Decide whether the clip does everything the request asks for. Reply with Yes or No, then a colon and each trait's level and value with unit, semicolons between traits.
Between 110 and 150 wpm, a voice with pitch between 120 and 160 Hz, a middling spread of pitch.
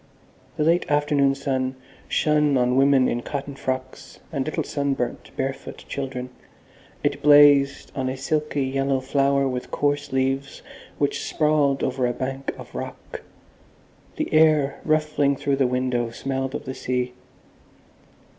No: slow, 135 wpm; low, 135 Hz; narrow, 1.7 semitones